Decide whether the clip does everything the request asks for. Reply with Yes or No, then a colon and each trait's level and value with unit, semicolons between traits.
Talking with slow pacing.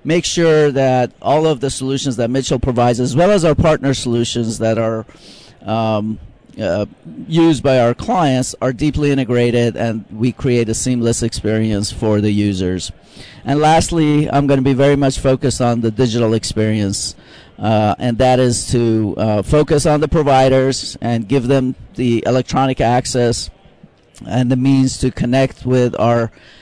No: average, 160 wpm